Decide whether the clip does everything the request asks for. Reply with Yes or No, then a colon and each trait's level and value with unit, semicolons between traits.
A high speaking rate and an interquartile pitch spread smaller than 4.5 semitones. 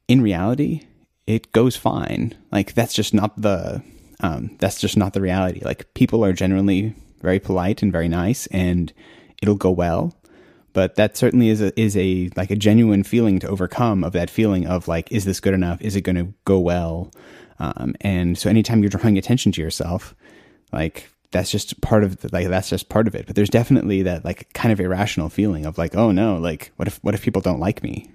Yes: fast, 215 wpm; average, 3.1 semitones